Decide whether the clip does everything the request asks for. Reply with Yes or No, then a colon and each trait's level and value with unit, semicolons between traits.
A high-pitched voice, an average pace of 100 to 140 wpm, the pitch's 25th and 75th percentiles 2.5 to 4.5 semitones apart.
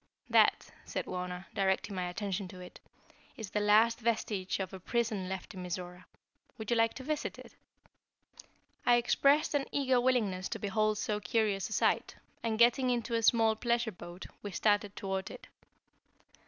No: high, 210 Hz; average, 170 wpm; average, 3.7 semitones